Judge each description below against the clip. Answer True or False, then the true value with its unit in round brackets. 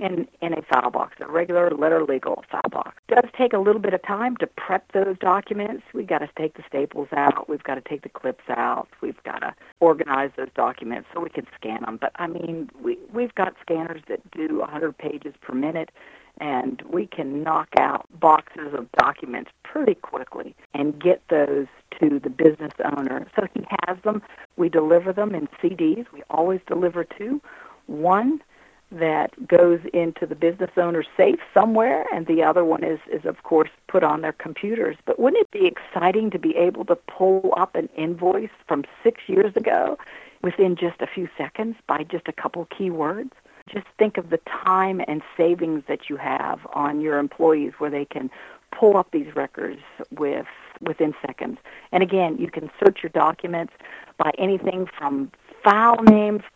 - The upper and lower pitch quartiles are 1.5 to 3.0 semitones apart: False (4.9 semitones)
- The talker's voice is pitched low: False (175 Hz)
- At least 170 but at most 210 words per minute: True (185 wpm)